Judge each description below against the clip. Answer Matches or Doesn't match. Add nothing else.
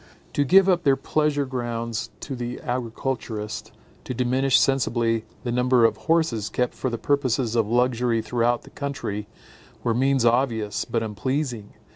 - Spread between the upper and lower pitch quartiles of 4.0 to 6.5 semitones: Doesn't match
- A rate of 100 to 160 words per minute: Matches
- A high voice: Doesn't match